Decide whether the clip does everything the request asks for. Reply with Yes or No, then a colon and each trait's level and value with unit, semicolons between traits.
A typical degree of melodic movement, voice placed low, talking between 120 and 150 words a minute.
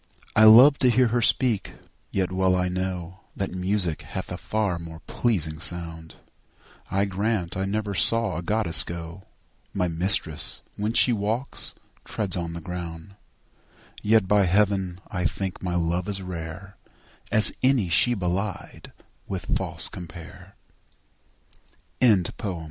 Yes: average, 3.4 semitones; very low, 95 Hz; average, 140 wpm